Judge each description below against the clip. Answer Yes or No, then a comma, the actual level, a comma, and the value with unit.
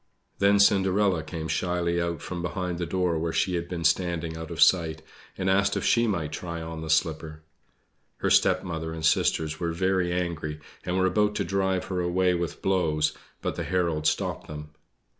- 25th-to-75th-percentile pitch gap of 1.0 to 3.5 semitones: Yes, narrow, 2.5 semitones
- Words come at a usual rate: Yes, average, 185 wpm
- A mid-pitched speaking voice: No, very low, 85 Hz